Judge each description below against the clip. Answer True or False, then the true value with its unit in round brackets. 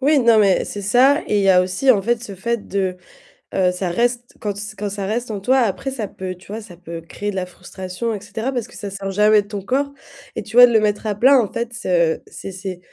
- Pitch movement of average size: True (3.7 semitones)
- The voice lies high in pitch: True (205 Hz)